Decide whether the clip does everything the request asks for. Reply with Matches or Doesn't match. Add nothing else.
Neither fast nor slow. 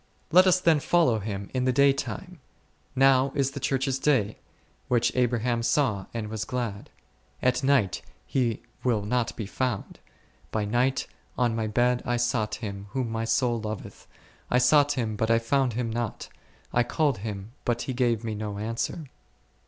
Matches